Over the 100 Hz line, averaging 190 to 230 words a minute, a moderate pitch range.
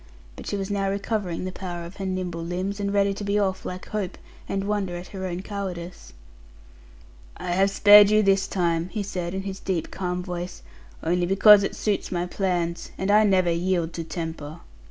No: high, 190 Hz; average, 195 wpm; narrow, 2.3 semitones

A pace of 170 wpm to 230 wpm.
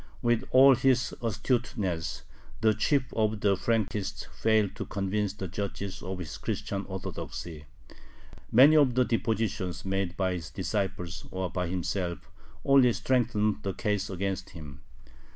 No: slow, 135 wpm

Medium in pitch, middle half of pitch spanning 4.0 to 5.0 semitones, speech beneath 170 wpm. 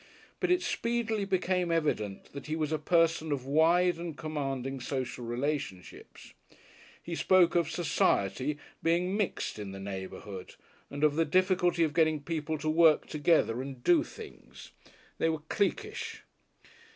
Yes: medium, 160 Hz; average, 4.6 semitones; average, 145 wpm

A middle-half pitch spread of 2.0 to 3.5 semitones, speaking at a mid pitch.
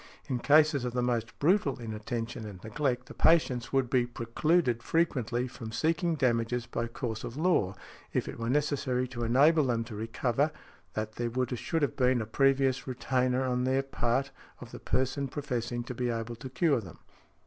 No: average, 2.8 semitones; low, 125 Hz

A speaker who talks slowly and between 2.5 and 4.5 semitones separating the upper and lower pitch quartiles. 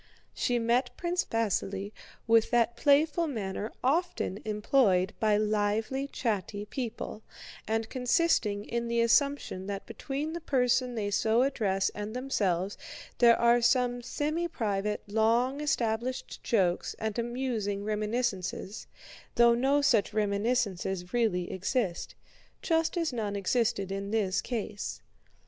Yes: slow, 120 wpm; average, 3.7 semitones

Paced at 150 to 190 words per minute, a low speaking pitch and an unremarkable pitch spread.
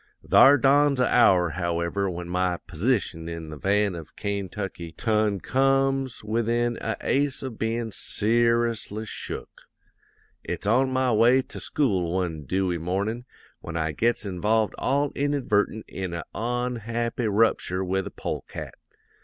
No: slow, 135 wpm; low, 110 Hz; average, 5.0 semitones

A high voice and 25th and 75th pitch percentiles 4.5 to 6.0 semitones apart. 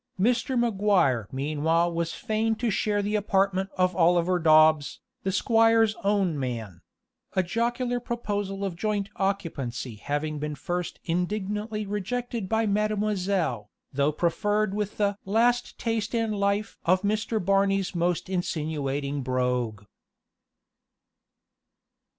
Yes: high, 195 Hz; average, 5.1 semitones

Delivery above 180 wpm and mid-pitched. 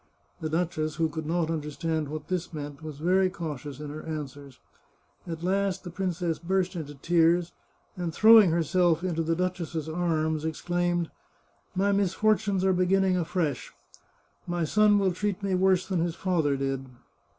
No: average, 160 wpm; medium, 170 Hz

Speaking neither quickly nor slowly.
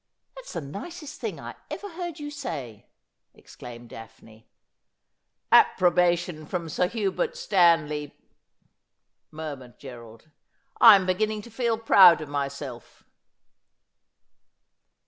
No: slow, 115 wpm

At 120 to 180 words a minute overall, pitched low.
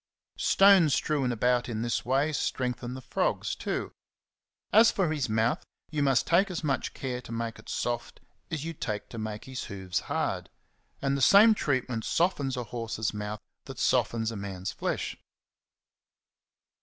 Yes: average, 160 wpm; low, 125 Hz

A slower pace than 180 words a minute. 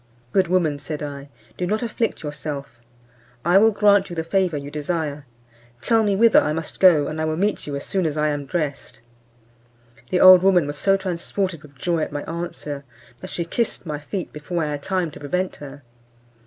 No: fast, 205 wpm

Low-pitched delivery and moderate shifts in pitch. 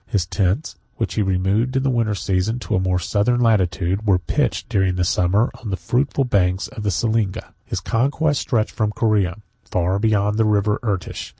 Yes: low, 105 Hz; average, 3.5 semitones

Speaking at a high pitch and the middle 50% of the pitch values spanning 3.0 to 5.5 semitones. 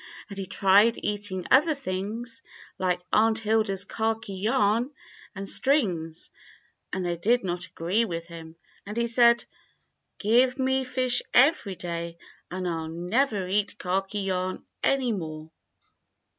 Yes: high, 205 Hz; average, 4.6 semitones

